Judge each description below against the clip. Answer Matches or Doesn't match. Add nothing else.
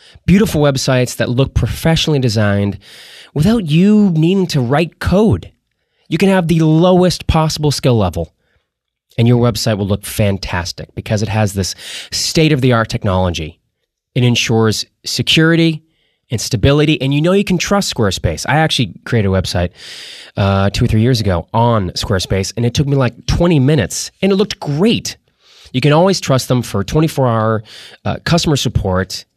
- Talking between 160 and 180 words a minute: Matches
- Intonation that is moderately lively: Doesn't match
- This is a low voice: Matches